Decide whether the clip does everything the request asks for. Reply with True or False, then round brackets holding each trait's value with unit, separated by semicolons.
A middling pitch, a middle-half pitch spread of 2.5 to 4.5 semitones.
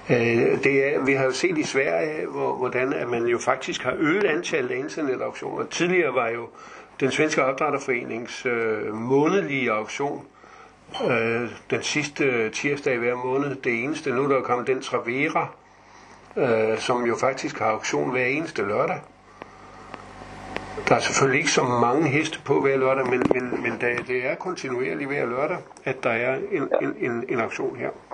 False (125 Hz; 2.9 semitones)